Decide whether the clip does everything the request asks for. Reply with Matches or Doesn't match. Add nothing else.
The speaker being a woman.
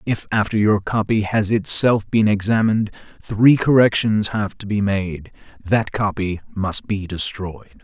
Doesn't match